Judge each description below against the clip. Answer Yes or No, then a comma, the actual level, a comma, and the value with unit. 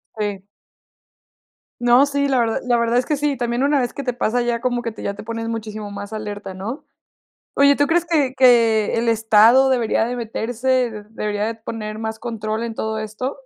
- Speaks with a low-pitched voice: No, high, 230 Hz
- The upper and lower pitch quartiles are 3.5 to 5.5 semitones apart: No, average, 2.7 semitones